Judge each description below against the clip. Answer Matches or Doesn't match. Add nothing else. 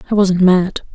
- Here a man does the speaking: Doesn't match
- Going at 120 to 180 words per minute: Doesn't match